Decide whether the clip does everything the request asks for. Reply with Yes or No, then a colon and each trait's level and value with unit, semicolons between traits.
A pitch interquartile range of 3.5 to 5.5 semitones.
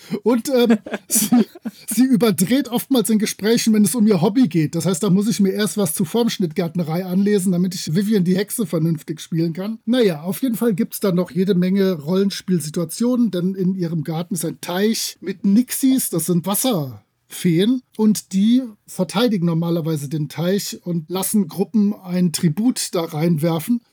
Yes: average, 4.2 semitones